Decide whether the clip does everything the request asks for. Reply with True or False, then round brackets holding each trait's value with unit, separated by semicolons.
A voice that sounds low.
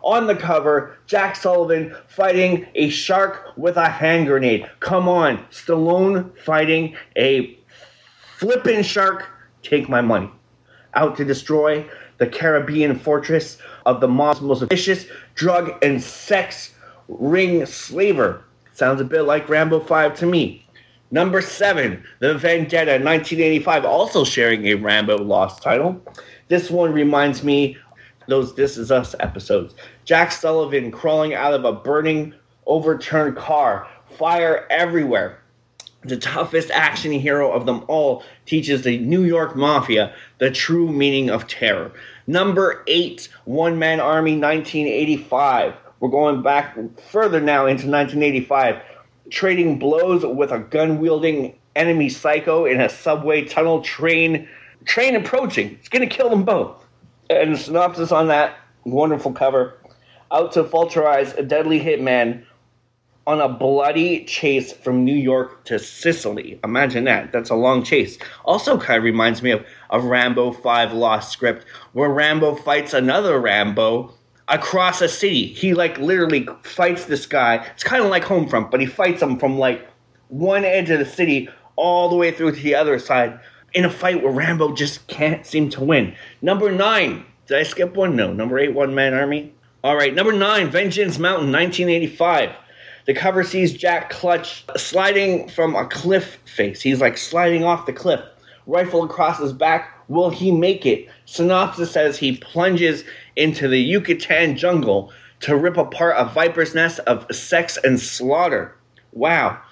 False (155 Hz)